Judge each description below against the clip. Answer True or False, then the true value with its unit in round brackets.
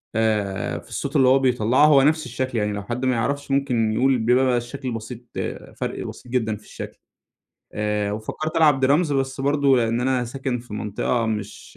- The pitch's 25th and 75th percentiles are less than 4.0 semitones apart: True (3.4 semitones)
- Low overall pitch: True (125 Hz)